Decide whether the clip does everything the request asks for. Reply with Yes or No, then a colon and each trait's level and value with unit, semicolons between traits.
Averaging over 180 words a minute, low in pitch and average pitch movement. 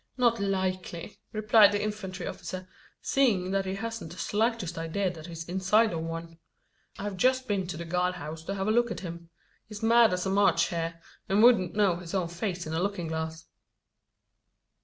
No: average, 190 wpm; high, 190 Hz; average, 3.7 semitones